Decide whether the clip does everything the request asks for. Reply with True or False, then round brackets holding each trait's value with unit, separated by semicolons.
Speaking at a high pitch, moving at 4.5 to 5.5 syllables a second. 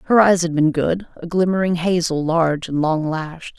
False (170 Hz; 4.8 syllables/s)